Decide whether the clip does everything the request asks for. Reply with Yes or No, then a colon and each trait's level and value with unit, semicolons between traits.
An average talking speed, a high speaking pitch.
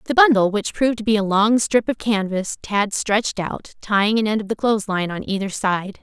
No: fast, 240 wpm; high, 210 Hz